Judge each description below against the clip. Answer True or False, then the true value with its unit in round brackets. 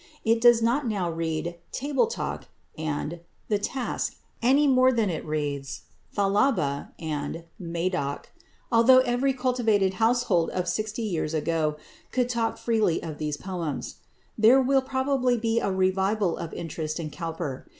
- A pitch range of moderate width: False (6.9 semitones)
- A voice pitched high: True (195 Hz)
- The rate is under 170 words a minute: True (140 wpm)